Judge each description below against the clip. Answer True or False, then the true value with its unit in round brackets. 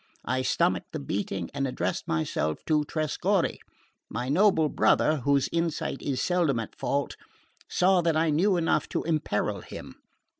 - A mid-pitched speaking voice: True (150 Hz)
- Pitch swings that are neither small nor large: True (4.7 semitones)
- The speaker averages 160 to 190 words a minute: False (150 wpm)